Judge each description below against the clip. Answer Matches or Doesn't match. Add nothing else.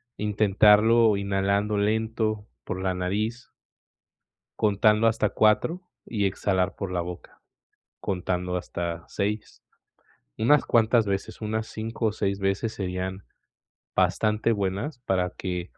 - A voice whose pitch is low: Matches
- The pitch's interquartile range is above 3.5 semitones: Doesn't match